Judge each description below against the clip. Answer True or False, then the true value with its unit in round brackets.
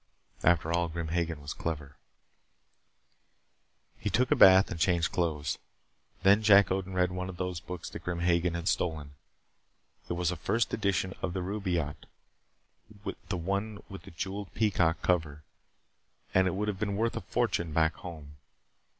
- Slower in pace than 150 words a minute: False (160 wpm)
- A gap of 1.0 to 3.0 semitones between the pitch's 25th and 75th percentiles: True (2.7 semitones)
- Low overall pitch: True (90 Hz)